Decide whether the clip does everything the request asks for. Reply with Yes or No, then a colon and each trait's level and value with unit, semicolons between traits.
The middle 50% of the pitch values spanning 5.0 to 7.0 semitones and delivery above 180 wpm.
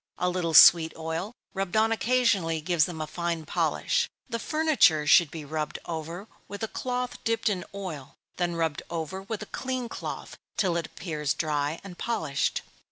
No: wide, 5.4 semitones; average, 170 wpm